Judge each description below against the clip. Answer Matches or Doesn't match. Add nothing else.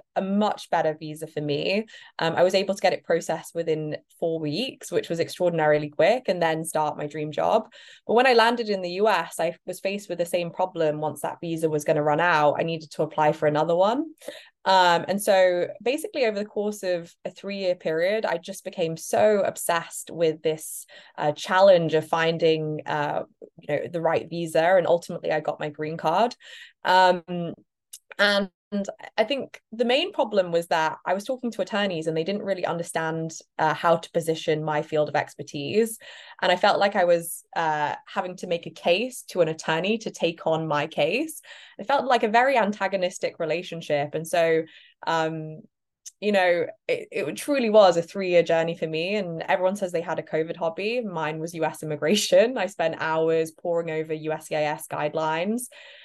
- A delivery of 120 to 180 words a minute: Doesn't match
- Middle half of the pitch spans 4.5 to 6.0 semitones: Doesn't match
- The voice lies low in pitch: Doesn't match